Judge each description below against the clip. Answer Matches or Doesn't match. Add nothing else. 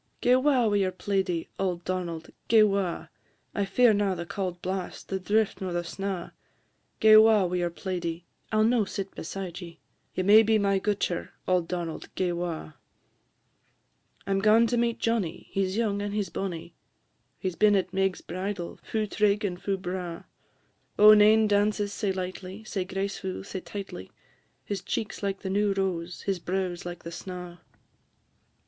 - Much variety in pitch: Doesn't match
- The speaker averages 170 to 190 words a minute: Matches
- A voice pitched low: Doesn't match